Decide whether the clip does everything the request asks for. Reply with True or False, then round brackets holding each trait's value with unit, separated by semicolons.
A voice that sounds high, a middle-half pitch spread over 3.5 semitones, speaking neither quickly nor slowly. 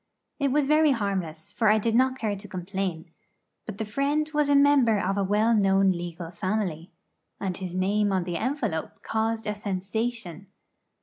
True (205 Hz; 4.0 semitones; 175 wpm)